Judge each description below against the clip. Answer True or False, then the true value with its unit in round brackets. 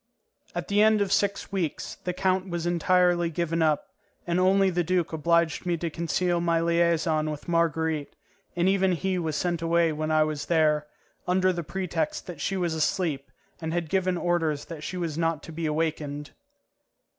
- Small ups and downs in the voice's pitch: True (2.3 semitones)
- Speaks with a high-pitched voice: False (170 Hz)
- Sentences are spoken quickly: False (180 wpm)